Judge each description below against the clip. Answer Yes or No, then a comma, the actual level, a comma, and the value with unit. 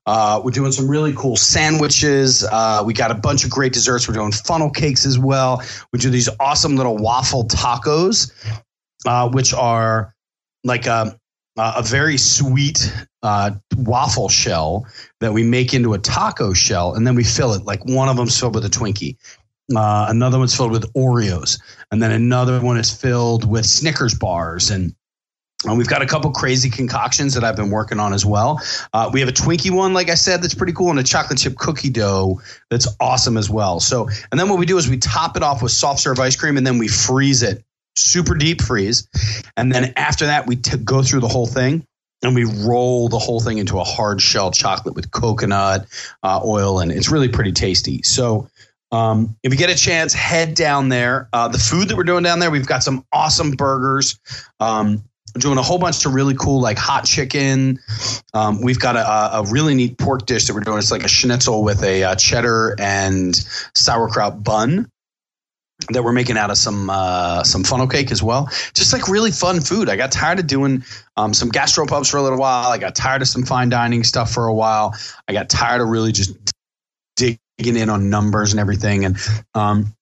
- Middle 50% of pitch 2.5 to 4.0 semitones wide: Yes, average, 3.7 semitones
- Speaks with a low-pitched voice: Yes, low, 120 Hz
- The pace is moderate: No, fast, 210 wpm